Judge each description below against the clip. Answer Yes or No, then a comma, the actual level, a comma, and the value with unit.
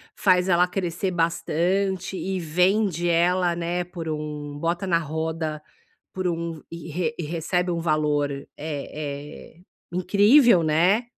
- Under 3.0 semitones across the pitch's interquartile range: Yes, narrow, 2.6 semitones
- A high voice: No, medium, 170 Hz